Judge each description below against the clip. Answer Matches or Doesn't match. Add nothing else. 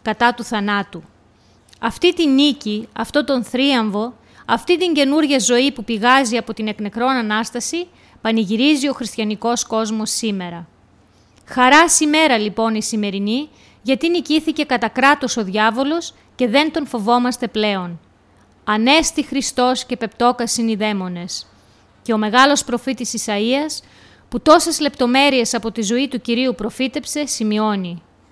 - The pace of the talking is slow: Doesn't match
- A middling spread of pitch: Matches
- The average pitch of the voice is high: Matches